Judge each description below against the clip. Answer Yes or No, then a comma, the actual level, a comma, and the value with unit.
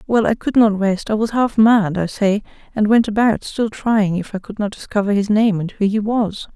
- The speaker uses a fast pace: Yes, fast, 245 wpm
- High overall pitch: Yes, high, 210 Hz